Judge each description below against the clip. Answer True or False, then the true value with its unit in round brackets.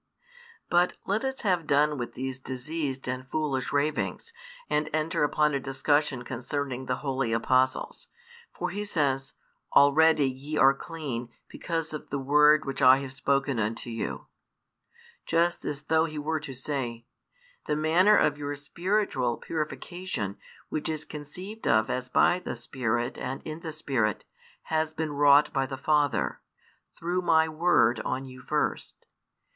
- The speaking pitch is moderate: True (145 Hz)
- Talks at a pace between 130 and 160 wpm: True (150 wpm)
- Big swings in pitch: False (3.3 semitones)